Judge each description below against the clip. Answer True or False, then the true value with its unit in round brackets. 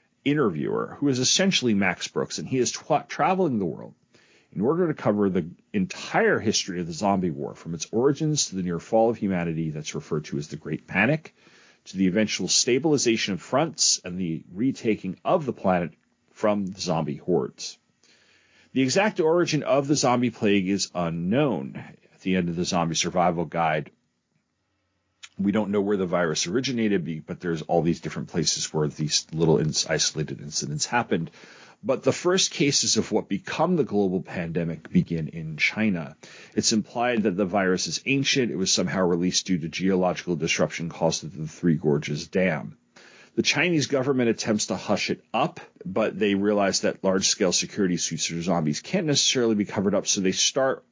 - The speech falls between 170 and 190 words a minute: True (180 wpm)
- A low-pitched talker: True (100 Hz)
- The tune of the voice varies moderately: False (6.0 semitones)